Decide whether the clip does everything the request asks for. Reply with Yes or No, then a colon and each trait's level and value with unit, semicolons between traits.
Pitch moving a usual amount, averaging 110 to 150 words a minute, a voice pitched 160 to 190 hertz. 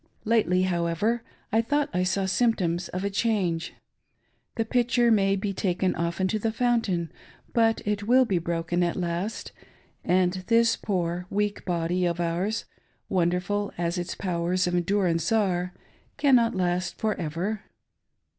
Yes: average, 3.9 semitones; average, 145 wpm; medium, 185 Hz